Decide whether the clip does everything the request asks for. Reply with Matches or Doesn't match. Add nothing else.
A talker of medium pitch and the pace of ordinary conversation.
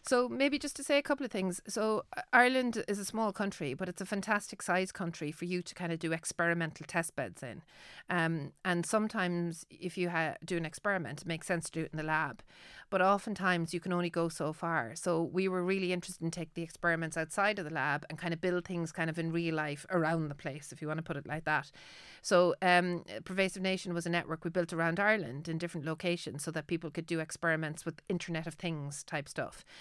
Doesn't match